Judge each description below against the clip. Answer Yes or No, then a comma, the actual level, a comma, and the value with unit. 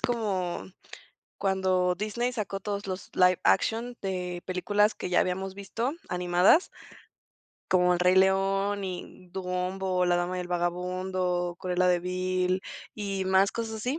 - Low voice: No, medium, 185 Hz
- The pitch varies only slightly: Yes, narrow, 1.7 semitones